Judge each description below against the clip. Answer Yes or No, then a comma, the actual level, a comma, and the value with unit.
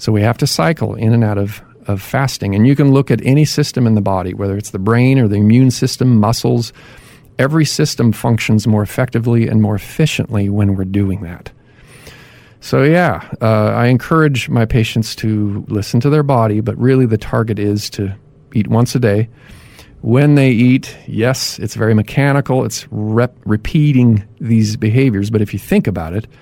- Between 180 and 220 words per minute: Yes, average, 185 wpm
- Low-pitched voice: Yes, low, 115 Hz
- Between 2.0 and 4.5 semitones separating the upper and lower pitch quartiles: Yes, average, 3.7 semitones